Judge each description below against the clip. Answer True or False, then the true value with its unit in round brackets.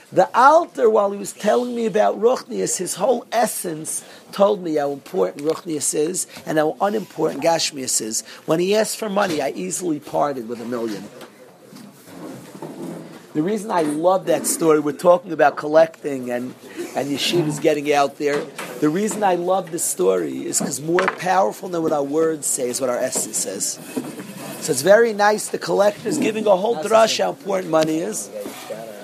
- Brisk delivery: False (175 wpm)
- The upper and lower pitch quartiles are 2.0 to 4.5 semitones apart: False (5.5 semitones)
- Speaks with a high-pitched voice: False (165 Hz)